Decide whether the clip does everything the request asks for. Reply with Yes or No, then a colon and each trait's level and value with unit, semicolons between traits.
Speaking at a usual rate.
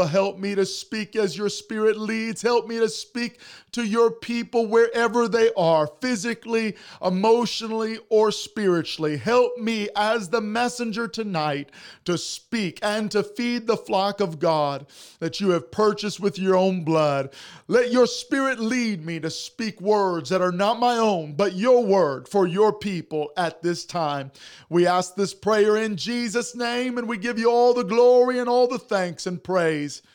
Yes: average, 175 wpm